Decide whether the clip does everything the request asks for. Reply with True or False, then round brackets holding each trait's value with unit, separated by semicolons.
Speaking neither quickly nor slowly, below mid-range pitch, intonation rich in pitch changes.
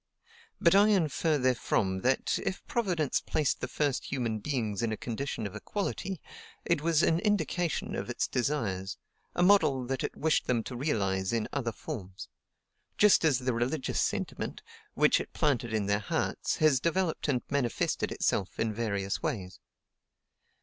True (155 wpm; 130 Hz; 6.3 semitones)